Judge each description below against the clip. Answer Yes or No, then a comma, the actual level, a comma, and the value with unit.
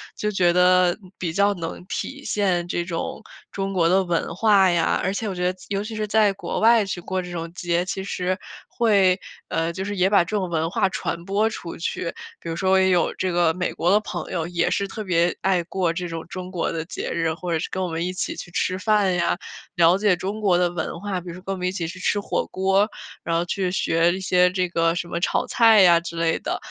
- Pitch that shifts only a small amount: Yes, narrow, 2.2 semitones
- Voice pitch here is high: No, medium, 180 Hz